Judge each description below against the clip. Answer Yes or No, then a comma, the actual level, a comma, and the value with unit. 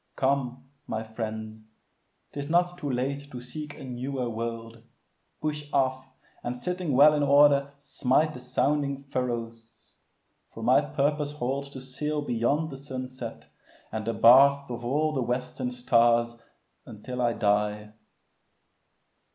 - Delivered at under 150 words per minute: Yes, slow, 135 wpm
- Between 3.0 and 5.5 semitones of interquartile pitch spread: Yes, average, 3.5 semitones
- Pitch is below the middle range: Yes, low, 130 Hz